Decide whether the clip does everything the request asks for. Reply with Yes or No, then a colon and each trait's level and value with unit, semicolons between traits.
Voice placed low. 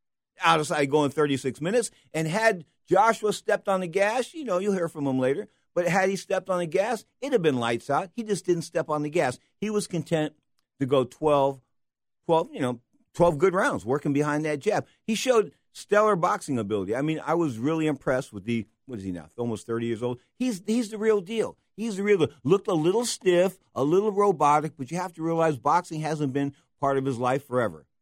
No: medium, 160 Hz